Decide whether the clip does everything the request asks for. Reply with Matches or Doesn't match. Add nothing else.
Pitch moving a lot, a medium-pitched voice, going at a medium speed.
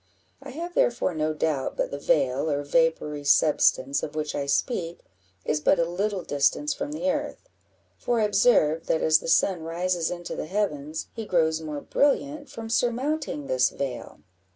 Matches